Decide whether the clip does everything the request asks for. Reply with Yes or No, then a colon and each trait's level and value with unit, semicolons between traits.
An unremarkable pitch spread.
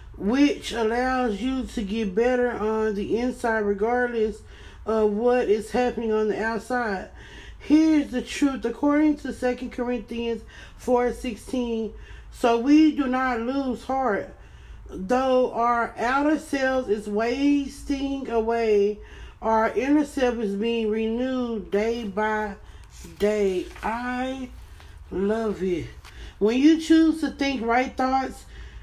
Yes: average, 3.0 semitones